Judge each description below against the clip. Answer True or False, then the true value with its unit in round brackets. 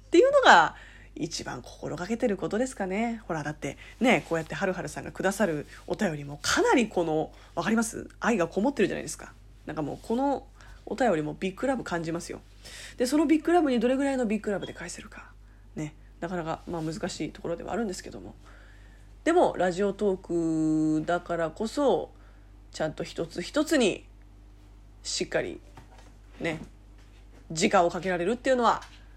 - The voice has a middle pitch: True (170 Hz)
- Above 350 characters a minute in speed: True (370 characters per minute)